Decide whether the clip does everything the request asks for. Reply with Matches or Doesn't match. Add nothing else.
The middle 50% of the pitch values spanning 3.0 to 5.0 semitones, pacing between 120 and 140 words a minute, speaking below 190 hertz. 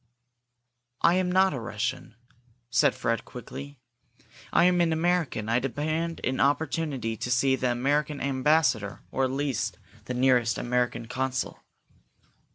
Matches